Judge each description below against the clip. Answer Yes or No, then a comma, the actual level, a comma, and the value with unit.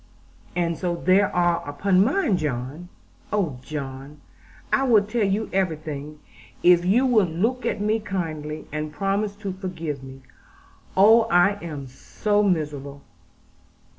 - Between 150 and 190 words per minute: No, slow, 135 wpm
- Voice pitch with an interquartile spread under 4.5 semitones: No, average, 5.1 semitones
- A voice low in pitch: No, medium, 175 Hz